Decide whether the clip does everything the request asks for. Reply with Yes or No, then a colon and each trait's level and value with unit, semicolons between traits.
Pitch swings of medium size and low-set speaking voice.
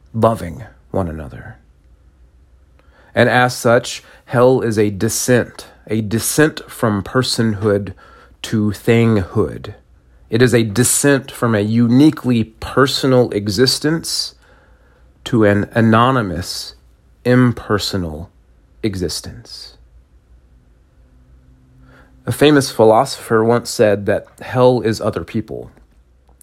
No: wide, 9.0 semitones; low, 110 Hz